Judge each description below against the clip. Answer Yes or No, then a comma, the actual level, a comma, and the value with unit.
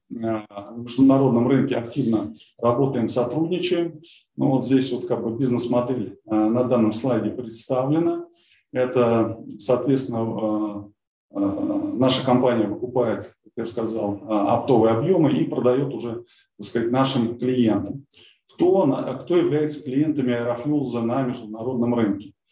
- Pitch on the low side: Yes, low, 125 Hz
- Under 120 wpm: Yes, slow, 110 wpm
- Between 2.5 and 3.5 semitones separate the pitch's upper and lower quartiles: Yes, average, 2.9 semitones